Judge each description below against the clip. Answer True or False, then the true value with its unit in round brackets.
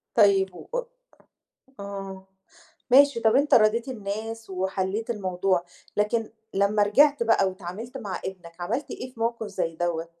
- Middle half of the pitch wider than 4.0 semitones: False (3.5 semitones)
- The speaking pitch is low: False (205 Hz)